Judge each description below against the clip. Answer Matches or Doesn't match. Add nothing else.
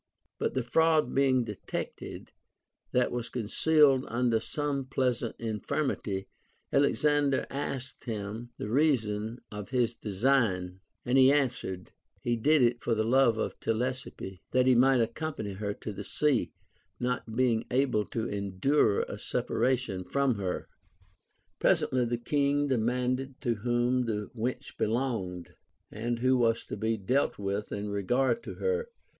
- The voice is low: Matches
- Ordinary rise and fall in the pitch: Matches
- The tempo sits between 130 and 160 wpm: Matches